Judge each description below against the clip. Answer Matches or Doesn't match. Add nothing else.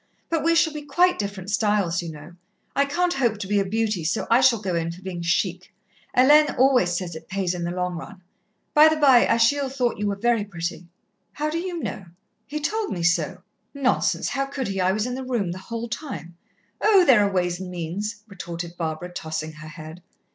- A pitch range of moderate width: Doesn't match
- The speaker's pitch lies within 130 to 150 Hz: Doesn't match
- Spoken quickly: Matches